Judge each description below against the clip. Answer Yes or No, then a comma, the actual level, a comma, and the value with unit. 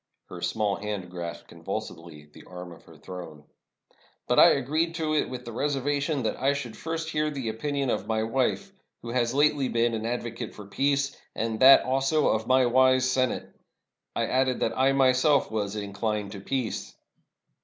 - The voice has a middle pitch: No, low, 125 Hz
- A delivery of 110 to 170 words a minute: No, average, 180 wpm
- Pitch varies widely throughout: No, average, 4.2 semitones